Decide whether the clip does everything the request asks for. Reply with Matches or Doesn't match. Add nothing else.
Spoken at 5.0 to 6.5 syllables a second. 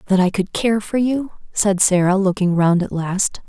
Doesn't match